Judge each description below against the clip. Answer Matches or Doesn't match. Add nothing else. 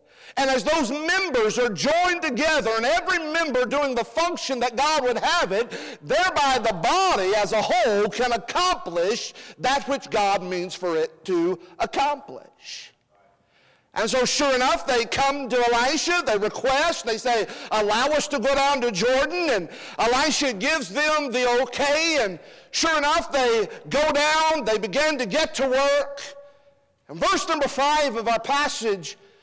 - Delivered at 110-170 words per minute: Matches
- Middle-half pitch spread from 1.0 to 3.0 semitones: Doesn't match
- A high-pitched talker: Matches